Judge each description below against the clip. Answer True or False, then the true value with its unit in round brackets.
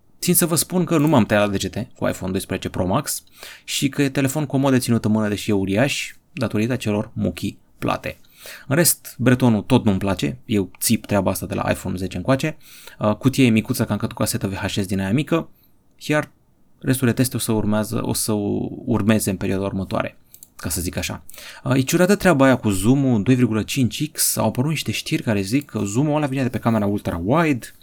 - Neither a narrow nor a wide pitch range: True (4.7 semitones)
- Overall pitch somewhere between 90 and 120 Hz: True (115 Hz)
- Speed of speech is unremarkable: False (205 wpm)